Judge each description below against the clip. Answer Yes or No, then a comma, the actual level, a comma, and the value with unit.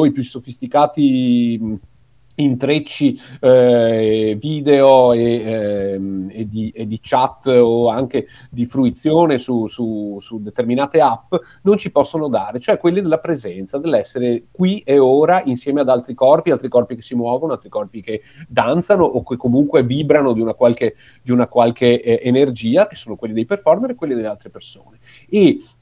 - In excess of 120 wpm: Yes, average, 165 wpm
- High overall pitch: No, low, 125 Hz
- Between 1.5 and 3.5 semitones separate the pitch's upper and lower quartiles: No, average, 4.0 semitones